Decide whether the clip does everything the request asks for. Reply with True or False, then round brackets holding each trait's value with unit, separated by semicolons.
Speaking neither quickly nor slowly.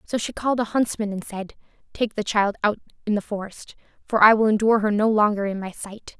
False (235 wpm)